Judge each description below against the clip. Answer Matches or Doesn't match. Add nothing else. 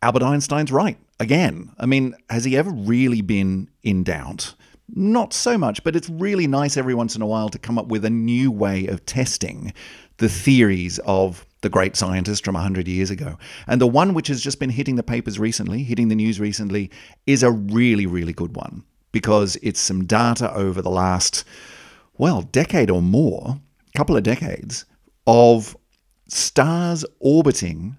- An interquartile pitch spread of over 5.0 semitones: Matches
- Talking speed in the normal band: Matches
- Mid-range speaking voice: Doesn't match